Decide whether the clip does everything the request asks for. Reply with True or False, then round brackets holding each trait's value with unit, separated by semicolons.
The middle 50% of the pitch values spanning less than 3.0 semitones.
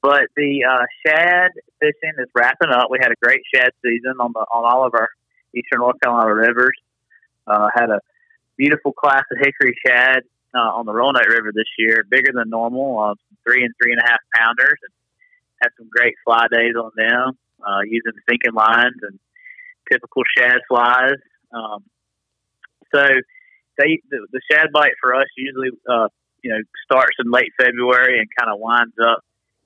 False (4.3 semitones)